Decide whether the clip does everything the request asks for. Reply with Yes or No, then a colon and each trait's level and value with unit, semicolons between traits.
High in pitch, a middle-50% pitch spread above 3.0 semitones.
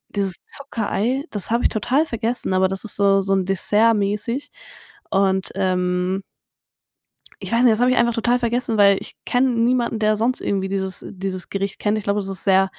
Yes: high, 205 Hz; average, 3.4 semitones